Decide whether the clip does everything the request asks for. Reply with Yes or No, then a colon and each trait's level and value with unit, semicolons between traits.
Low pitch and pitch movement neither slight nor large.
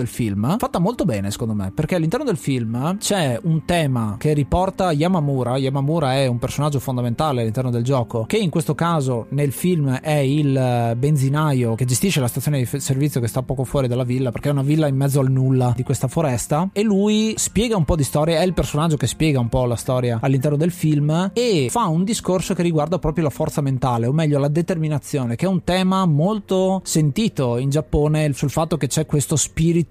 No: medium, 150 Hz; average, 4.3 semitones